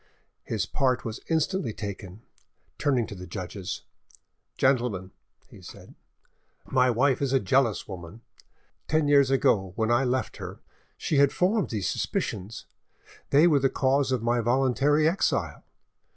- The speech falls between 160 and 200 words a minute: No, average, 140 wpm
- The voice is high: No, low, 125 Hz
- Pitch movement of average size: Yes, average, 4.6 semitones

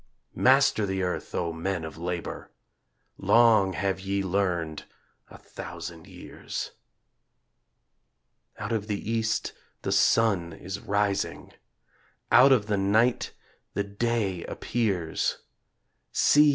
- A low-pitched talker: Yes, low, 100 Hz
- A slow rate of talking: Yes, slow, 110 wpm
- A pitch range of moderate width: Yes, average, 3.7 semitones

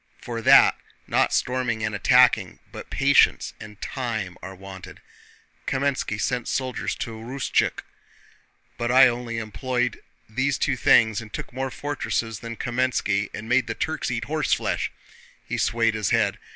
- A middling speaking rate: Yes, average, 145 wpm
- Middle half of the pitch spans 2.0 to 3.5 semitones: Yes, average, 2.8 semitones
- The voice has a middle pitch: No, low, 120 Hz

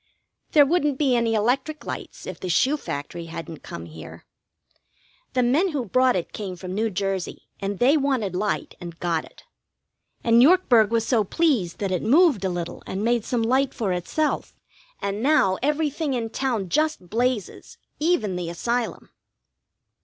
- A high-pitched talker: Yes, high, 230 Hz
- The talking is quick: No, average, 165 wpm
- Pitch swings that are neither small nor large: No, wide, 6.5 semitones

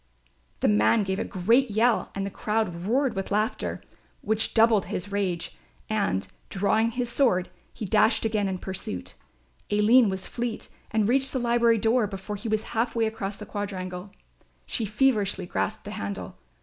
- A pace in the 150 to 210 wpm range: Yes, average, 165 wpm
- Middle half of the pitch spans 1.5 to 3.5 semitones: Yes, average, 3.0 semitones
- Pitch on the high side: Yes, high, 210 Hz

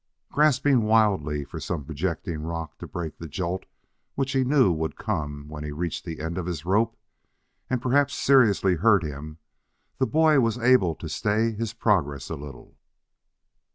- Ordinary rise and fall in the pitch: No, wide, 6.8 semitones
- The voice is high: No, very low, 90 Hz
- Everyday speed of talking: Yes, average, 165 wpm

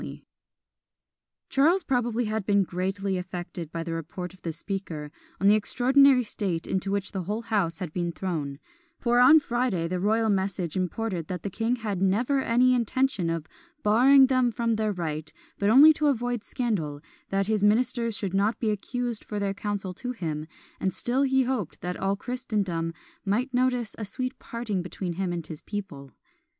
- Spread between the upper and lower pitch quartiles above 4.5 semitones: Yes, average, 5.1 semitones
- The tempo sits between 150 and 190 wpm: Yes, average, 180 wpm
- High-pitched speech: Yes, high, 205 Hz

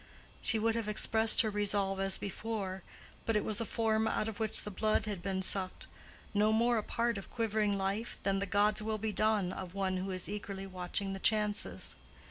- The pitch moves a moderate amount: No, narrow, 2.1 semitones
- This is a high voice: Yes, high, 210 Hz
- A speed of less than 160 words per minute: No, average, 195 wpm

